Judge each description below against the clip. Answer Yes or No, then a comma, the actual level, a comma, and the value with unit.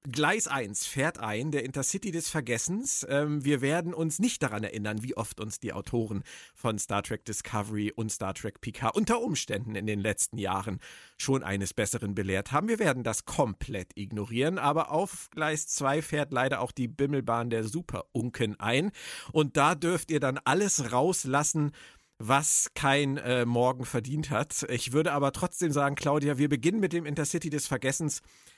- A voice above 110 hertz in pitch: Yes, low, 135 Hz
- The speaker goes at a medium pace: Yes, average, 170 wpm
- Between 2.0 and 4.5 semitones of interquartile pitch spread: No, average, 5.3 semitones